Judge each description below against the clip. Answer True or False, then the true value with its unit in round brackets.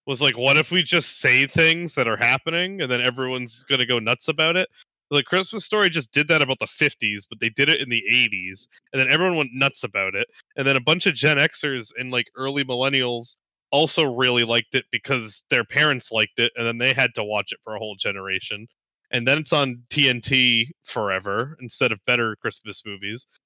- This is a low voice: True (130 Hz)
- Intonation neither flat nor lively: True (3.8 semitones)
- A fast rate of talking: True (215 wpm)